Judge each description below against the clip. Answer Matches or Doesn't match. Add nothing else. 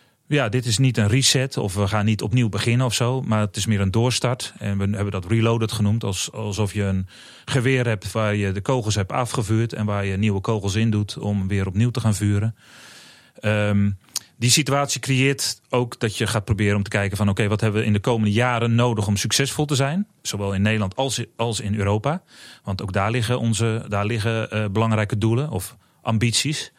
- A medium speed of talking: Doesn't match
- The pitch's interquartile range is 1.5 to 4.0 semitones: Matches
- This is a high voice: Doesn't match